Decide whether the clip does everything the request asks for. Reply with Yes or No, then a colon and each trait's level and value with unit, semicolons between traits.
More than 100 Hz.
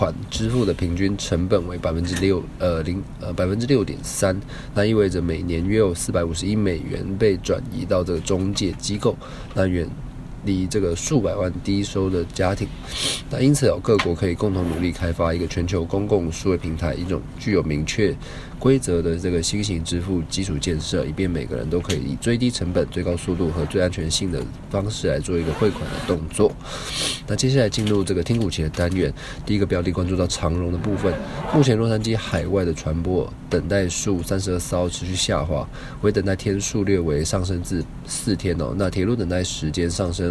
No: very low, 90 Hz